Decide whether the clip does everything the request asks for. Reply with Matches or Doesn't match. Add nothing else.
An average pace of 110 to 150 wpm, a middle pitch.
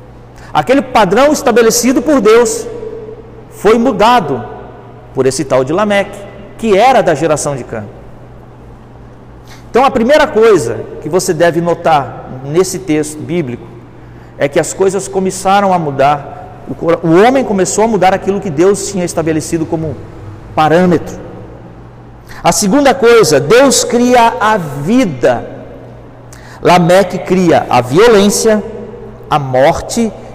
Matches